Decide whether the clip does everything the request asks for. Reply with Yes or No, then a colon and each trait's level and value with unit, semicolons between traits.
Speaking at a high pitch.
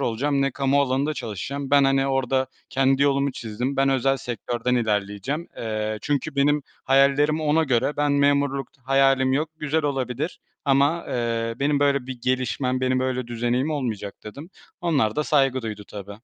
No: low, 135 Hz